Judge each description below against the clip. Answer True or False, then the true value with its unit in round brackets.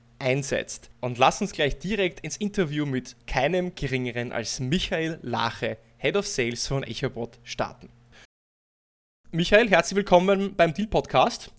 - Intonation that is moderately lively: False (7.1 semitones)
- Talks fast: False (135 wpm)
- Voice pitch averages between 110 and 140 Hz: True (135 Hz)